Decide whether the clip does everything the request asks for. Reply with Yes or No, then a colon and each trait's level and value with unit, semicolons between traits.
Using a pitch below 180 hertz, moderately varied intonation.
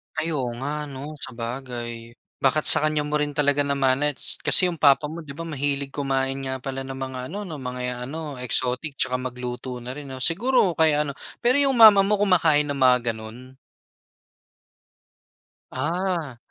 Yes: medium, 140 Hz; average, 3.3 semitones